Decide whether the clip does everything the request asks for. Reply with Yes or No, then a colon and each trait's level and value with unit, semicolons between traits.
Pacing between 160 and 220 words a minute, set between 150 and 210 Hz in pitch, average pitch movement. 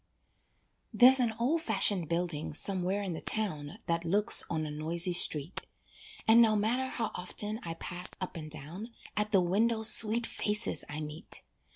Yes: average, 165 wpm; high, 190 Hz; average, 4.9 semitones